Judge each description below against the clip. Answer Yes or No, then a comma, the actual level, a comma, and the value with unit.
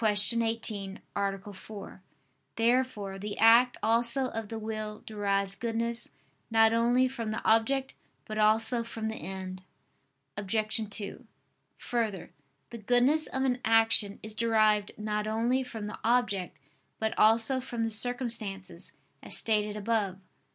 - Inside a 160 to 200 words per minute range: No, slow, 135 wpm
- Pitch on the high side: Yes, high, 220 Hz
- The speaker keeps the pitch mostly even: Yes, narrow, 2.0 semitones